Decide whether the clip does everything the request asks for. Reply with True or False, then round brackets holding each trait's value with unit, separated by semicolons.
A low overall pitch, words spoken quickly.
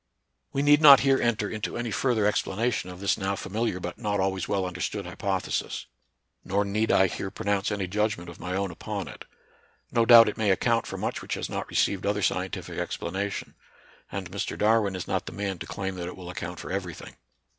True (100 Hz; 210 wpm)